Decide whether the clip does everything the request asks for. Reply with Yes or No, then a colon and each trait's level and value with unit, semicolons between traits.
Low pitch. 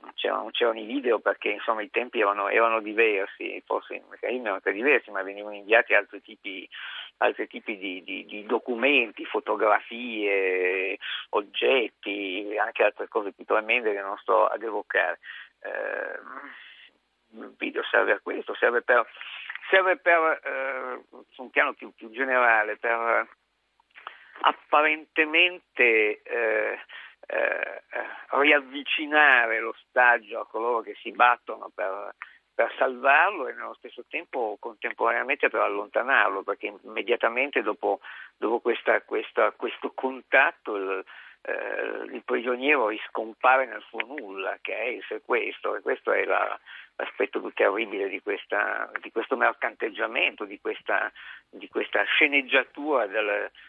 No: medium, 185 Hz